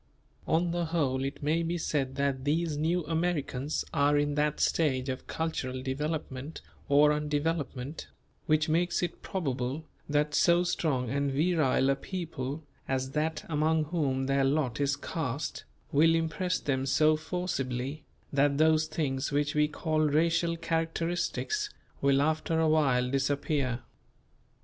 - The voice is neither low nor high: Yes, medium, 150 Hz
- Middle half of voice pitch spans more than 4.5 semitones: No, average, 2.9 semitones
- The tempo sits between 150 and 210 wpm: No, average, 140 wpm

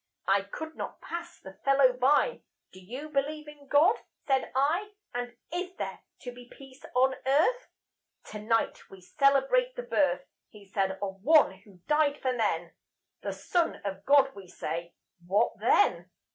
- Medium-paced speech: Yes, average, 160 wpm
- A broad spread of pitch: Yes, wide, 7.2 semitones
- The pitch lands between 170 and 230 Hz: No, very high, 265 Hz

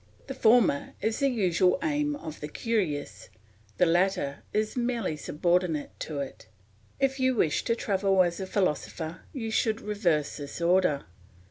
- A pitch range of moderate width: No, wide, 6.3 semitones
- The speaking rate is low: No, average, 150 wpm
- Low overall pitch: No, high, 190 Hz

